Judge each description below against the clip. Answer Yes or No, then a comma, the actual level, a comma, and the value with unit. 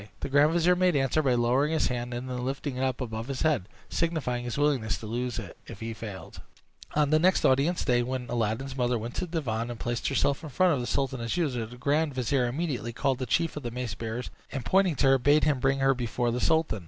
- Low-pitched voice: Yes, low, 130 Hz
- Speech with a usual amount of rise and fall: Yes, average, 3.5 semitones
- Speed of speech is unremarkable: No, fast, 250 wpm